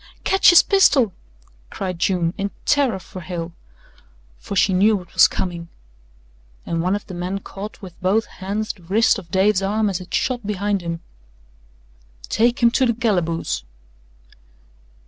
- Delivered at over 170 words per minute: No, average, 155 wpm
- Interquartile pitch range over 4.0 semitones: No, average, 3.3 semitones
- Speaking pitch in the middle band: No, high, 195 Hz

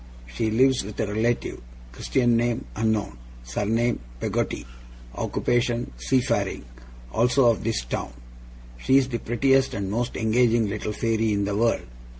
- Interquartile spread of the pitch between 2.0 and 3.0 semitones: Yes, narrow, 2.4 semitones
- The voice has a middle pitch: No, low, 115 Hz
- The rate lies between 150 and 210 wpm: No, average, 140 wpm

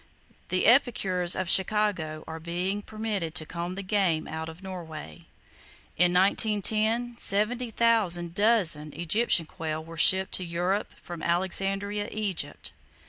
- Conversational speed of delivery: No, slow, 125 wpm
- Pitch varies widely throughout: No, average, 3.7 semitones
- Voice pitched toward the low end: No, medium, 185 Hz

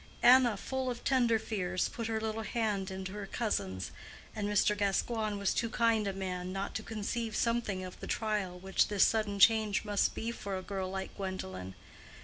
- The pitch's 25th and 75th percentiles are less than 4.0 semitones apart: Yes, average, 2.8 semitones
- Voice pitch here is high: Yes, high, 205 Hz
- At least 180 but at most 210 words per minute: Yes, average, 185 wpm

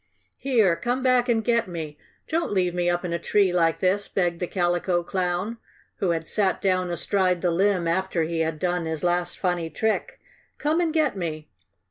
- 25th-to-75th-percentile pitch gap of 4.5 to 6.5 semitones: No, average, 3.2 semitones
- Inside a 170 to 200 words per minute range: Yes, average, 190 wpm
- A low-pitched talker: No, medium, 180 Hz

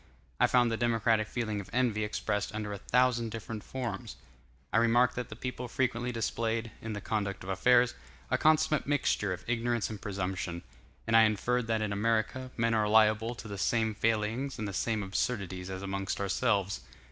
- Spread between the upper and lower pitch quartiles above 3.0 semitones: No, narrow, 2.6 semitones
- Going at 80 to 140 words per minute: No, average, 180 wpm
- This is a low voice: Yes, low, 110 Hz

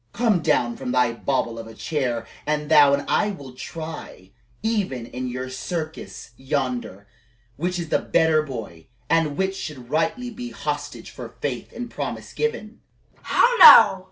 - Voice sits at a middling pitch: Yes, medium, 150 Hz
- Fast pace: No, average, 155 wpm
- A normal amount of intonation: No, wide, 6.1 semitones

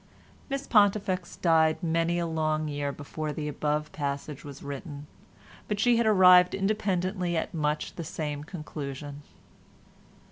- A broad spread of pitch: No, average, 3.8 semitones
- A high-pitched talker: No, medium, 160 Hz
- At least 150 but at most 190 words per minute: No, slow, 135 wpm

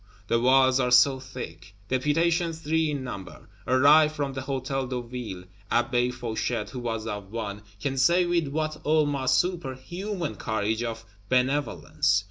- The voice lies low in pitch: Yes, low, 130 Hz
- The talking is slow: No, average, 145 wpm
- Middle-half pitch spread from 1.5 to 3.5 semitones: No, average, 4.0 semitones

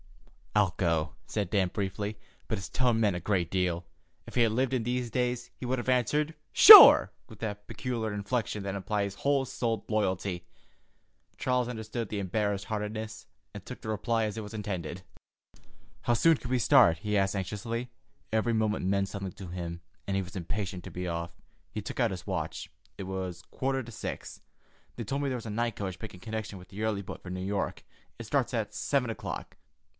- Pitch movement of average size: Yes, average, 3.6 semitones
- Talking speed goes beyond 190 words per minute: Yes, average, 200 wpm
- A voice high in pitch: No, low, 105 Hz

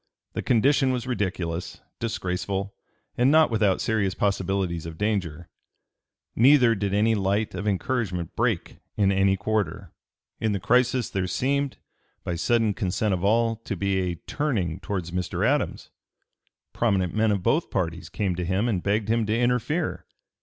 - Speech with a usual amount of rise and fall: Yes, average, 3.9 semitones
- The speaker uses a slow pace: No, average, 155 wpm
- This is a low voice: Yes, low, 100 Hz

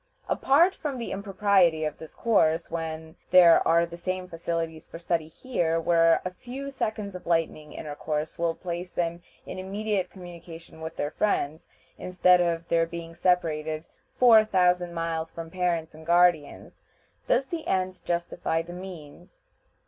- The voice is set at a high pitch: No, medium, 170 Hz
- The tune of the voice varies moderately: No, narrow, 2.2 semitones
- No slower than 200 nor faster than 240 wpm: No, average, 150 wpm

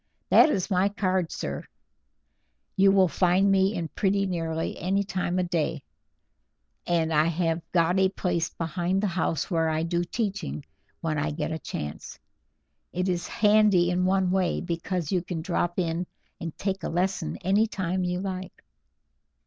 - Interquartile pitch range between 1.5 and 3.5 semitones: Yes, narrow, 2.4 semitones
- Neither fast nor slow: Yes, average, 165 wpm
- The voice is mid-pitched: Yes, medium, 180 Hz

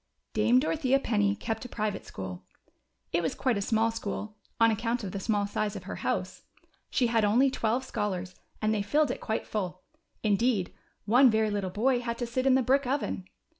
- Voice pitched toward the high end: Yes, high, 220 Hz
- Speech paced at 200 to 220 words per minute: Yes, fast, 205 wpm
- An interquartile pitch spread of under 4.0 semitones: Yes, average, 3.4 semitones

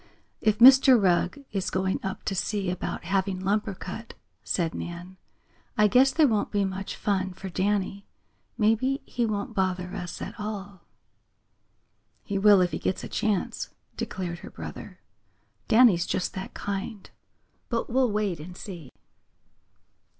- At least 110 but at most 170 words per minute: Yes, average, 145 wpm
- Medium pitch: No, high, 195 Hz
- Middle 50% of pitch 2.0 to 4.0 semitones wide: Yes, narrow, 2.5 semitones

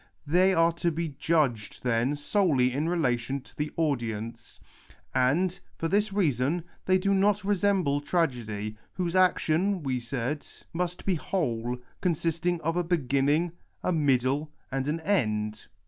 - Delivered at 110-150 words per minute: Yes, average, 140 wpm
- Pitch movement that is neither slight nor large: No, wide, 5.8 semitones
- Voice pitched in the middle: Yes, medium, 155 Hz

